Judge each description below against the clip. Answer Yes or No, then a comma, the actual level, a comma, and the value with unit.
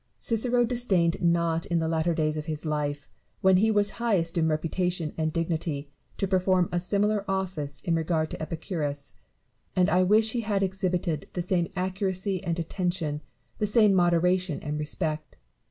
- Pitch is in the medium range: Yes, medium, 175 Hz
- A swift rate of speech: No, average, 165 wpm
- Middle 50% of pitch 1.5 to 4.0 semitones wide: Yes, average, 3.2 semitones